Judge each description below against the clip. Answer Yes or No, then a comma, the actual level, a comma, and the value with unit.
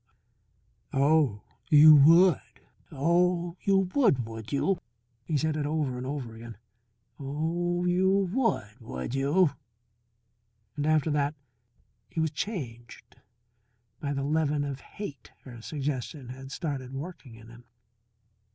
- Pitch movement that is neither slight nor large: Yes, average, 4.2 semitones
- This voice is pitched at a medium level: Yes, medium, 145 Hz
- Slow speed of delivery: Yes, slow, 125 wpm